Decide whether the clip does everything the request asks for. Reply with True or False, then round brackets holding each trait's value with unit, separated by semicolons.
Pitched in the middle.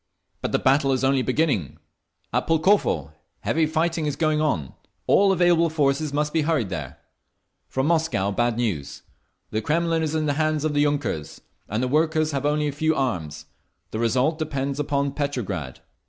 True (145 Hz)